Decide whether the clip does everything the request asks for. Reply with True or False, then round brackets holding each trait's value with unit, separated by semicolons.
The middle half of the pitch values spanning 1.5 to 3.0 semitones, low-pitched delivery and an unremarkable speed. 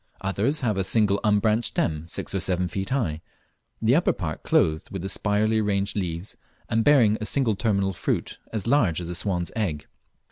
False (3.6 semitones; 100 Hz; 185 wpm)